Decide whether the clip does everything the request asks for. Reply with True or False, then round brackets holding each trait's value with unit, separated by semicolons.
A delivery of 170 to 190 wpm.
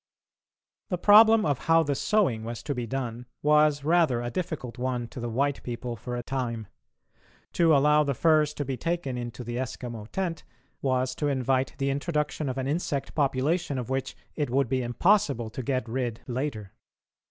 True (180 wpm)